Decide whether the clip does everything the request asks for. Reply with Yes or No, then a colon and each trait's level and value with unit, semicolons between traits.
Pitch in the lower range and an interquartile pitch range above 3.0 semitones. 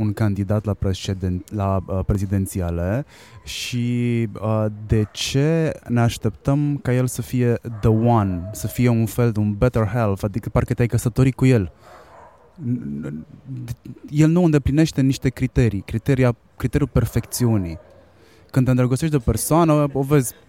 Yes: low, 115 Hz; average, 4.1 semitones